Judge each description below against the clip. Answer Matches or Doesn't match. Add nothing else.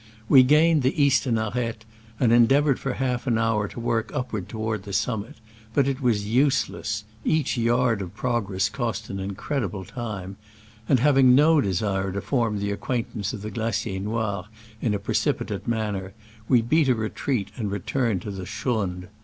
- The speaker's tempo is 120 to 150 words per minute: Doesn't match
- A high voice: Doesn't match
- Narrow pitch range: Doesn't match